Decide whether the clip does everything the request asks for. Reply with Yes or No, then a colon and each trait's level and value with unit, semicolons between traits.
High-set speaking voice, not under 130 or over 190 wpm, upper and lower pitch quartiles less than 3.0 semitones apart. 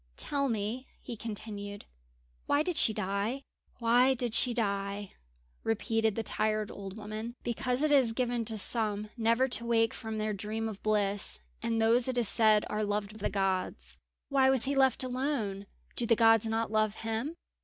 Yes: high, 225 Hz; average, 175 wpm; narrow, 2.5 semitones